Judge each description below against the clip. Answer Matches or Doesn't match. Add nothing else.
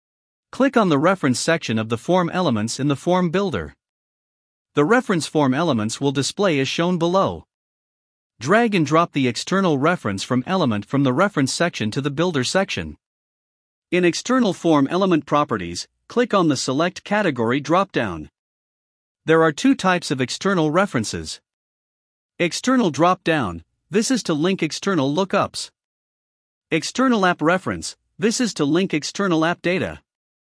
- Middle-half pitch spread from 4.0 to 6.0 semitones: Matches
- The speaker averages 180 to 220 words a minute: Doesn't match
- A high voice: Doesn't match